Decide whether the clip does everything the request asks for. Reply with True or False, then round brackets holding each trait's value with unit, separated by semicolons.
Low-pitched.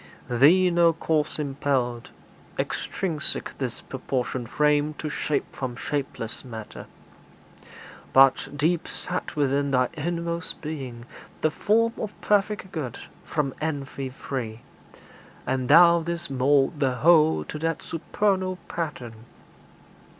False (150 Hz)